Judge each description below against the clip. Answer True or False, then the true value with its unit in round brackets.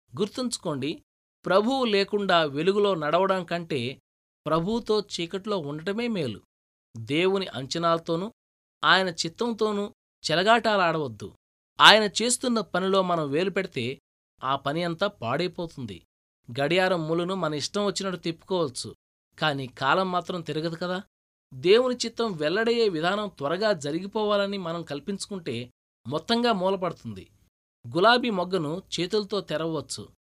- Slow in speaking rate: False (95 wpm)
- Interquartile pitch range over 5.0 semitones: True (5.4 semitones)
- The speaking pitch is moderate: True (180 Hz)